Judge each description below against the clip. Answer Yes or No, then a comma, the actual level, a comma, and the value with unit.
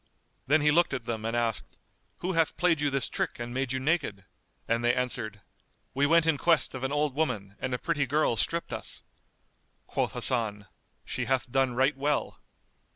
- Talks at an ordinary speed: Yes, average, 190 wpm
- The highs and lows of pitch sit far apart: No, average, 4.0 semitones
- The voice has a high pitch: No, low, 130 Hz